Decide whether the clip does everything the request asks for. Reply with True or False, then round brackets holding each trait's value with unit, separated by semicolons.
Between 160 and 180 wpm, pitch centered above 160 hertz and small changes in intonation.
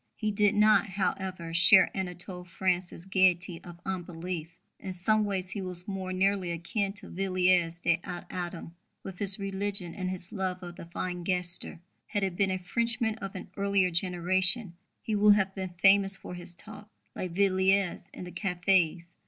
True (170 wpm; 185 Hz; 1.8 semitones)